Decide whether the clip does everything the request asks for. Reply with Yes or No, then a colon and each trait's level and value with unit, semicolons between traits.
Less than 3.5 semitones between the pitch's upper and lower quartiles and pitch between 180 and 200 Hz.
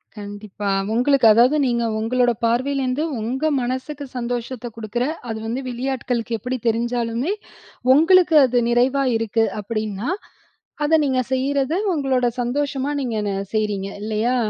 No: average, 3.0 semitones; high, 245 Hz